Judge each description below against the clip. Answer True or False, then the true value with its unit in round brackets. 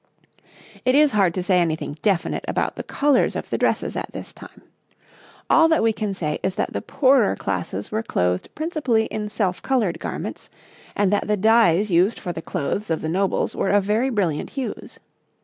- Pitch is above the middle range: True (205 Hz)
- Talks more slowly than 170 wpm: False (190 wpm)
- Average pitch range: True (5.0 semitones)